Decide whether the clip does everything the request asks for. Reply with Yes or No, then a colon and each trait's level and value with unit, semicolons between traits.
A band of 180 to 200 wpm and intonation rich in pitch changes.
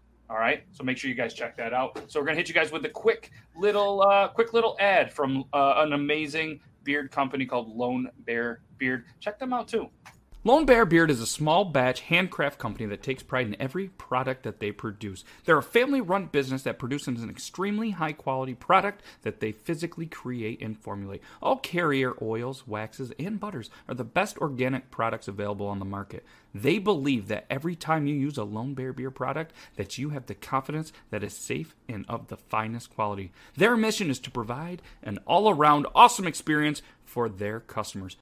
Yes: average, 195 wpm; wide, 6.2 semitones